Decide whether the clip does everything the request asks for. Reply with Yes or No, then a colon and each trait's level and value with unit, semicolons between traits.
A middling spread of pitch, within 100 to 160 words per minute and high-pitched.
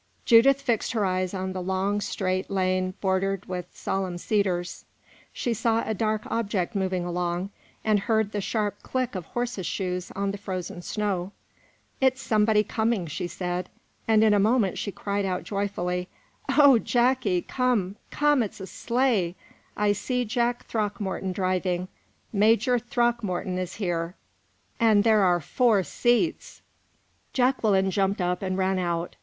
Yes: average, 3.5 semitones; average, 150 wpm; high, 200 Hz